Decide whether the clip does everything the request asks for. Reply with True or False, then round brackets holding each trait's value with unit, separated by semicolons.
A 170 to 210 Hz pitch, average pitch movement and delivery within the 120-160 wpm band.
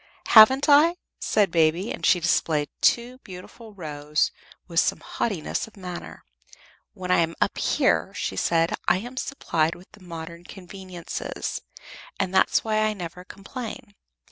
True (185 Hz; 4.4 semitones; 145 wpm)